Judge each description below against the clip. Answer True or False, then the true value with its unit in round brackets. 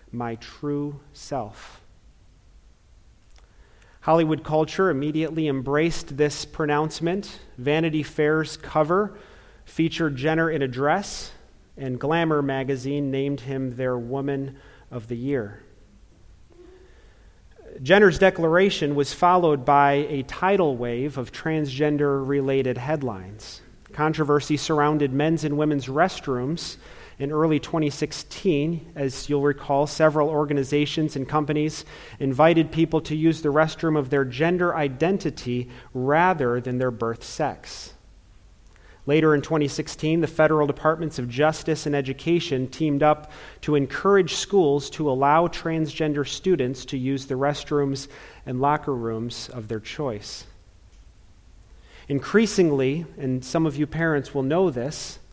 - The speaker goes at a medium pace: False (115 wpm)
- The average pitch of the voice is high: False (145 Hz)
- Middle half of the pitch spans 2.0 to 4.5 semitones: True (3.1 semitones)